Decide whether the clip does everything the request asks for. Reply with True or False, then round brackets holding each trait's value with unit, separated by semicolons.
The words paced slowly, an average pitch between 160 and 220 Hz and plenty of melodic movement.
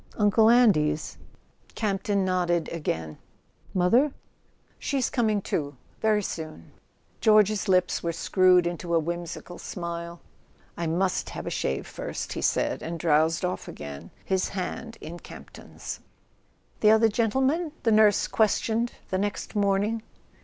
False (130 wpm; 185 Hz; 4.3 semitones)